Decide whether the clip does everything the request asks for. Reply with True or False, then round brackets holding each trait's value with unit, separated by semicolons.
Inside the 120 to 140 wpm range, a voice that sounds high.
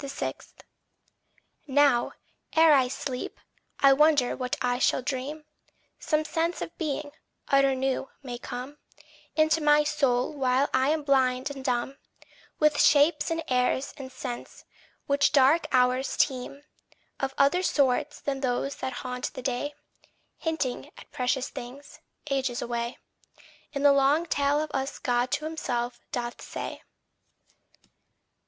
True (135 wpm; 275 Hz)